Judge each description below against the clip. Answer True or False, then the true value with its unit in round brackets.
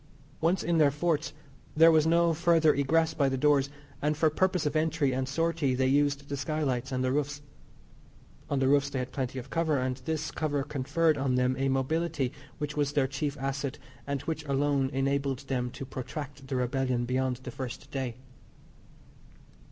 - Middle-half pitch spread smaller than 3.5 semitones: True (2.8 semitones)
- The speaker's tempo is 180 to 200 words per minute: True (185 wpm)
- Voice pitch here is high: False (140 Hz)